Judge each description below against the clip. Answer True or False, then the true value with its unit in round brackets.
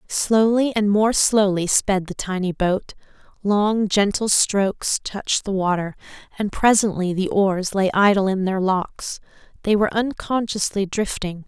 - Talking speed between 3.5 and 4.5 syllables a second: True (4.3 syllables/s)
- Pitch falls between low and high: False (200 Hz)